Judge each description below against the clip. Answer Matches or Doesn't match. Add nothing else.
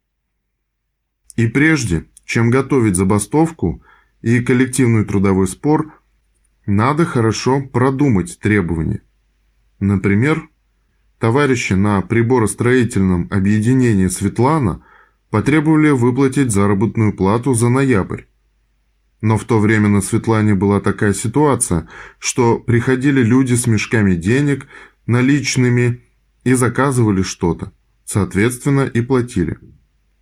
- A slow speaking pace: Matches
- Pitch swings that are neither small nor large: Matches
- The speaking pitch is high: Doesn't match